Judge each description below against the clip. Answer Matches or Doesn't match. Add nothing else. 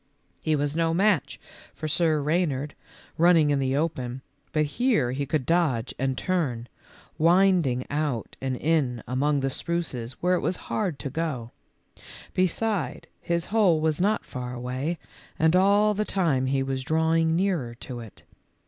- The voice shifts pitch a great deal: Doesn't match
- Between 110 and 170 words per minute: Matches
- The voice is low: Doesn't match